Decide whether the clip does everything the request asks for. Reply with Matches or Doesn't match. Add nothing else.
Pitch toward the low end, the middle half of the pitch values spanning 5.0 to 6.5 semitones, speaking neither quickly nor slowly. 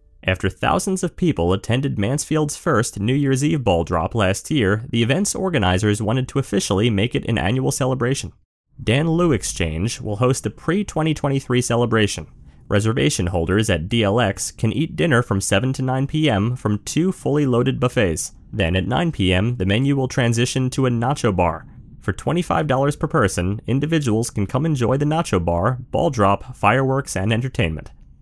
Matches